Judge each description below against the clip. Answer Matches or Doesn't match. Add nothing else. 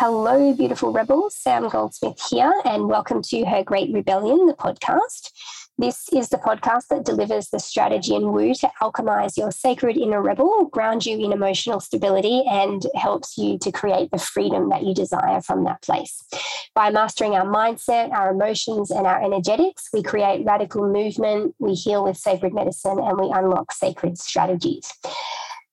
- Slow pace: Doesn't match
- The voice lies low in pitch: Doesn't match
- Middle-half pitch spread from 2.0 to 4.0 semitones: Doesn't match